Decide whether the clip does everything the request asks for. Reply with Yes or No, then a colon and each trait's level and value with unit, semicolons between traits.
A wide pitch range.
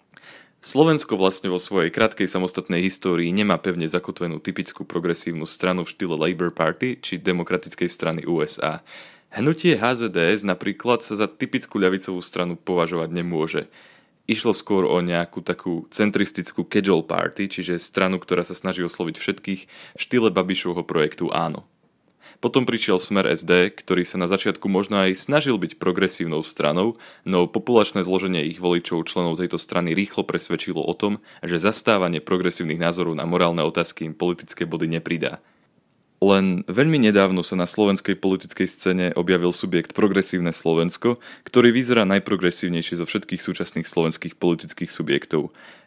No: narrow, 2.4 semitones